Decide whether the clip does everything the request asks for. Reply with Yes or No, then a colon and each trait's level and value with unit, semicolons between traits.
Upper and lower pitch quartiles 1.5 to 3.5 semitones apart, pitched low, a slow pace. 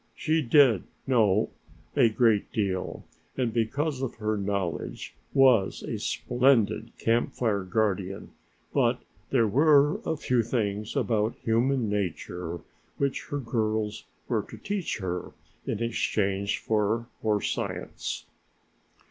No: average, 3.9 semitones; low, 110 Hz; slow, 120 wpm